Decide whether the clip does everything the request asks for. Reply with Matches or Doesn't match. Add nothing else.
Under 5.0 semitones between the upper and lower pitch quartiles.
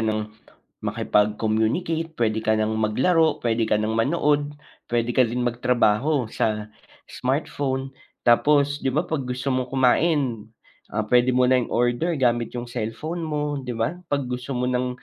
Matches